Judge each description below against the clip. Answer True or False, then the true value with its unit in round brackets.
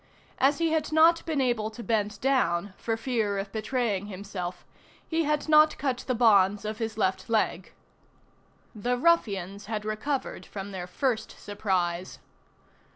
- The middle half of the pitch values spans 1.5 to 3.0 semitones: False (4.9 semitones)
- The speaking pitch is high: True (220 Hz)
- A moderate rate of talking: True (150 wpm)